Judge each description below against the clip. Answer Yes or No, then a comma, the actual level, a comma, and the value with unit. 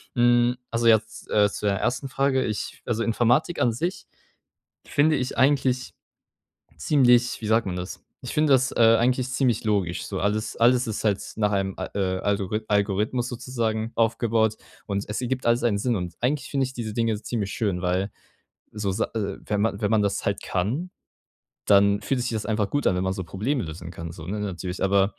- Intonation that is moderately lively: Yes, average, 3.6 semitones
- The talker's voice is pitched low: Yes, low, 110 Hz